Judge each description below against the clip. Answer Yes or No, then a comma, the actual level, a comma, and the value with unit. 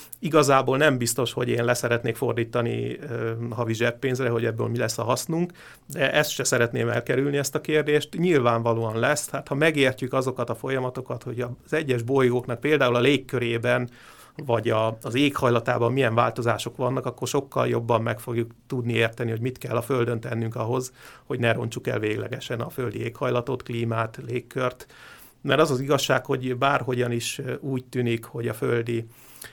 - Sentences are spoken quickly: Yes, fast, 165 wpm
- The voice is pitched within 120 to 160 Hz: Yes, low, 125 Hz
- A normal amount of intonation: No, narrow, 2.1 semitones